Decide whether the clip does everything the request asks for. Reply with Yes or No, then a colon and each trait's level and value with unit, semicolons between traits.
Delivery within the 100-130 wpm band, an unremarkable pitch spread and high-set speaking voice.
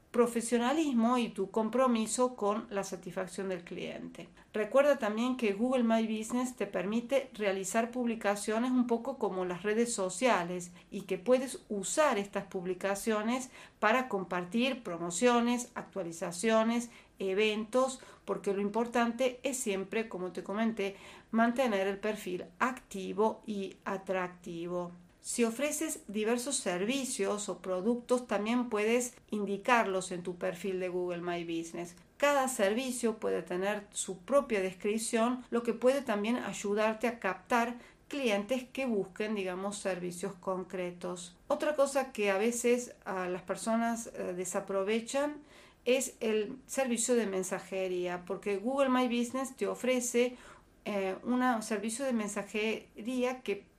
Yes: slow, 125 wpm; average, 4.2 semitones; high, 215 Hz